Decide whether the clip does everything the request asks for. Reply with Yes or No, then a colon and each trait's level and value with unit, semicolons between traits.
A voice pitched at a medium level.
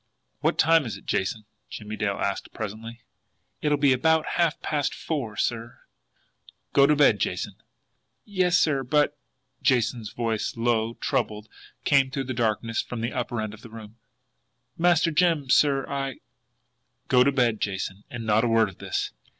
No: low, 120 Hz